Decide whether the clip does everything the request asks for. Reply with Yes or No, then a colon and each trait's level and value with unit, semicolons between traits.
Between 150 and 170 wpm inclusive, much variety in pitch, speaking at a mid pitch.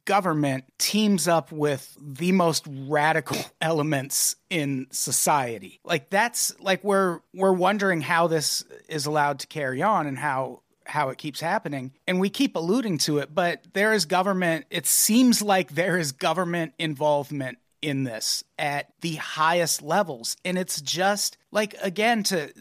No: average, 155 wpm; average, 4.8 semitones; medium, 165 Hz